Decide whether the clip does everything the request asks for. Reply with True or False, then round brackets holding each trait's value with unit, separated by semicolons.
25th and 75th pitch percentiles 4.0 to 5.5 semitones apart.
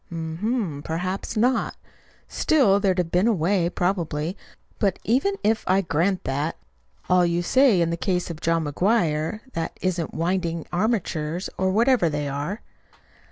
False (3.6 semitones)